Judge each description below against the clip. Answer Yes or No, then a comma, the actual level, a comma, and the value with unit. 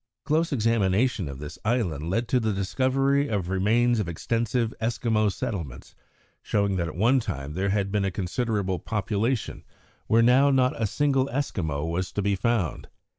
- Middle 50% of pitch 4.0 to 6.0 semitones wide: Yes, average, 4.5 semitones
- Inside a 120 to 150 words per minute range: No, average, 165 wpm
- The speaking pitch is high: No, low, 105 Hz